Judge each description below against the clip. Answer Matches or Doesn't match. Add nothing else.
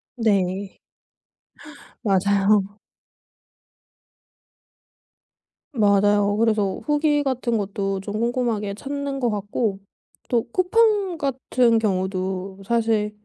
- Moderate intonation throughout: Matches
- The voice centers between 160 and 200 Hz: Doesn't match